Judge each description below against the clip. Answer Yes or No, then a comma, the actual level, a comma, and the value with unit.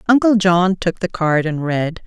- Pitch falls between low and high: Yes, medium, 180 Hz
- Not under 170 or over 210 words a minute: Yes, fast, 205 wpm